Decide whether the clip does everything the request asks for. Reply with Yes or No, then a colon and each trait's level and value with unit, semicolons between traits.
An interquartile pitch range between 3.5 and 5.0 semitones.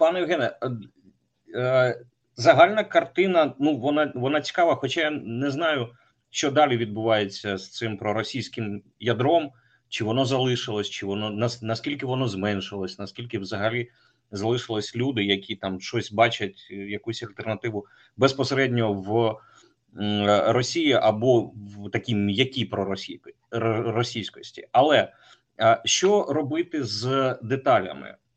Yes: average, 4.3 semitones